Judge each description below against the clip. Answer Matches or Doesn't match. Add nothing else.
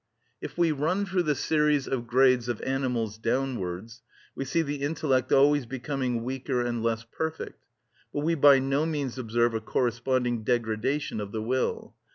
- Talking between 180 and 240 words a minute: Doesn't match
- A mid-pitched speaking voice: Doesn't match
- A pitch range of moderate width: Matches